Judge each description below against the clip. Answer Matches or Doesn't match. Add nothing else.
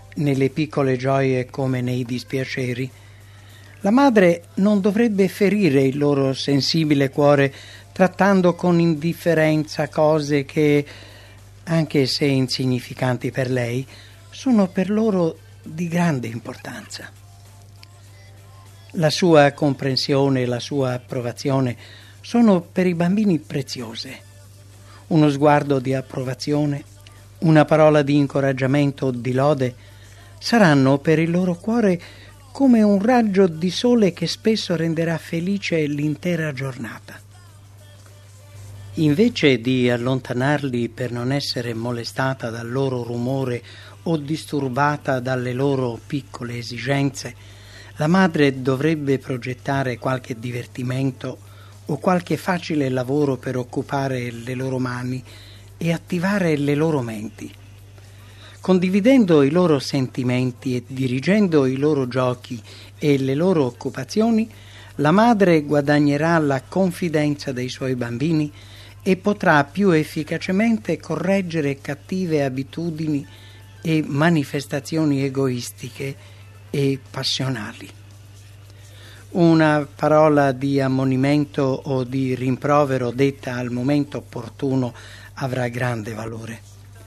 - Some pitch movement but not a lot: Matches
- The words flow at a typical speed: Doesn't match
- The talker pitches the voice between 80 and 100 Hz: Doesn't match